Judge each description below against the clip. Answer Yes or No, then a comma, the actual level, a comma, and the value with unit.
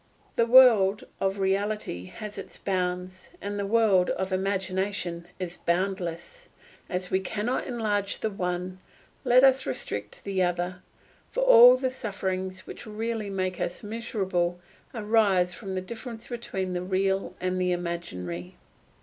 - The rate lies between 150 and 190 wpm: No, slow, 135 wpm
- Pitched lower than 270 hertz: Yes, high, 190 Hz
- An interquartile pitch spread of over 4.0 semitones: No, average, 3.2 semitones